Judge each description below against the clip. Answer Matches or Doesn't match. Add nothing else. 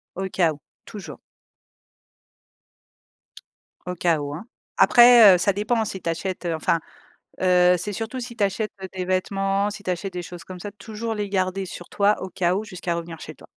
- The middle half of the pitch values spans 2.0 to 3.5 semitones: Matches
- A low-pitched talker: Doesn't match